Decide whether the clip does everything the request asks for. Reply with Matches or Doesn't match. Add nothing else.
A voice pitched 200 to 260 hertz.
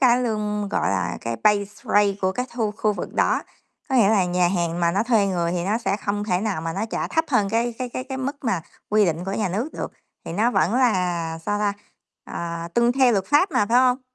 Matches